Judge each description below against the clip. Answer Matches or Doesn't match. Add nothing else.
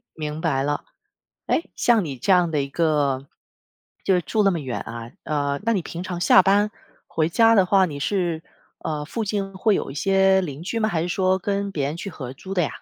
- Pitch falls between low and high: Matches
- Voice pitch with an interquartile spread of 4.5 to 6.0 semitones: Matches